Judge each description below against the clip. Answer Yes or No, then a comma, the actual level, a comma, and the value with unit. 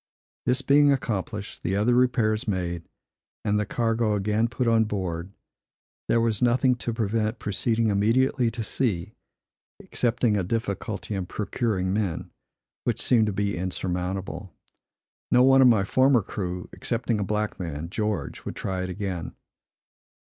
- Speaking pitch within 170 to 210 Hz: No, low, 105 Hz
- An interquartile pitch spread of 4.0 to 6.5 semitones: No, average, 3.4 semitones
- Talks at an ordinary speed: Yes, average, 145 wpm